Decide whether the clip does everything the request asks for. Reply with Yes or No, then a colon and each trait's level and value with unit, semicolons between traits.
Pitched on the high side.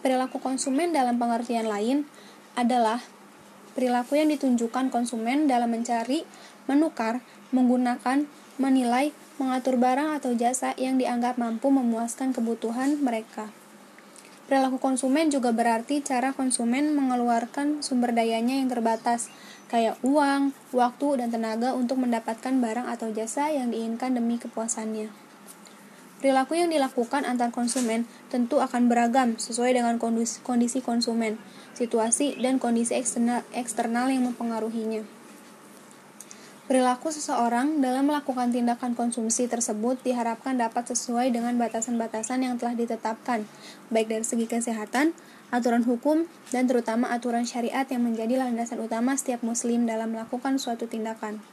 Yes: high, 245 Hz